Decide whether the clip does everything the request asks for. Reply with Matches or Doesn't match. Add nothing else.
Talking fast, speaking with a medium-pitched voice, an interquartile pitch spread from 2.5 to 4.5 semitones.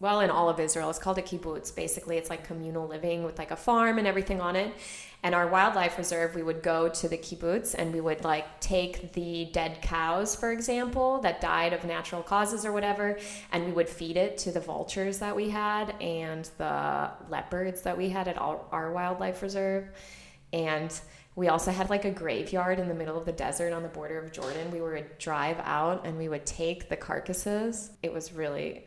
Matches